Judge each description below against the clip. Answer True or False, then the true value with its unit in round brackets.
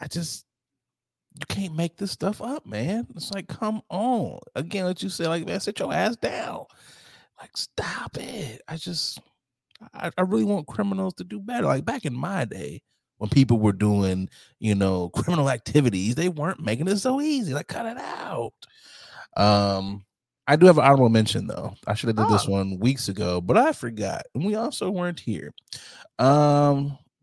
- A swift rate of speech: False (185 wpm)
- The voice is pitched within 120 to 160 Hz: True (140 Hz)